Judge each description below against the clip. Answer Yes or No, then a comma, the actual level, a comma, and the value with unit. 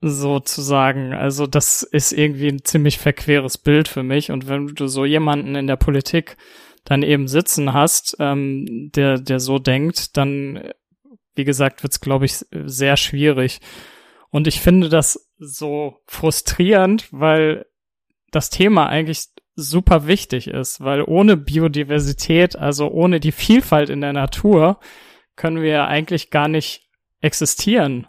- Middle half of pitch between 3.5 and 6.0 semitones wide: No, narrow, 2.4 semitones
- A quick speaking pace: No, average, 140 wpm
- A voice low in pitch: No, medium, 150 Hz